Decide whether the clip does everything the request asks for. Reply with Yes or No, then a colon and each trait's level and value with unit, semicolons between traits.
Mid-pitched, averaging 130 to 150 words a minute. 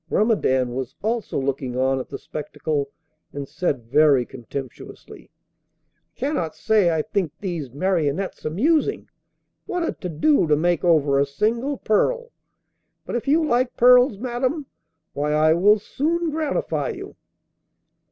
Yes: medium, 175 Hz; average, 140 wpm